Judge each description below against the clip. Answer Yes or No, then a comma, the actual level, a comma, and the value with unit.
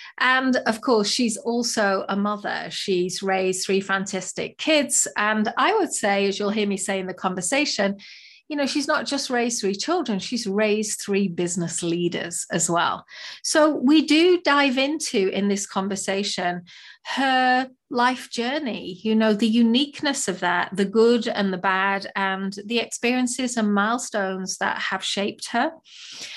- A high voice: Yes, high, 210 Hz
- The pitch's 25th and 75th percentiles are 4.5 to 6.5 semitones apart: Yes, average, 4.8 semitones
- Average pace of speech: Yes, average, 160 wpm